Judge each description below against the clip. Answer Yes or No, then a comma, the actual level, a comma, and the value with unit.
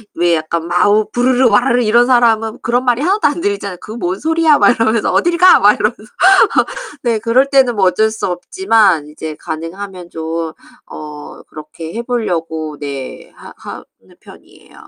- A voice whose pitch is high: Yes, high, 215 Hz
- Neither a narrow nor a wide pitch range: No, wide, 6.4 semitones